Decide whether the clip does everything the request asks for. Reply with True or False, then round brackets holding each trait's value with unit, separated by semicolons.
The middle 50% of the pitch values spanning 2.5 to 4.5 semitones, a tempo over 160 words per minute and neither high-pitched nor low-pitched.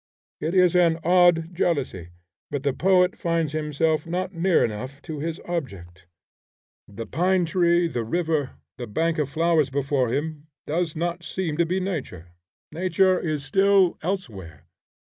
False (4.0 semitones; 145 wpm; 160 Hz)